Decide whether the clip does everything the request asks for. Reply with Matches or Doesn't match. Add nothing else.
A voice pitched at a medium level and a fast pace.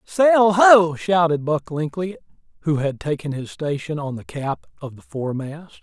Doesn't match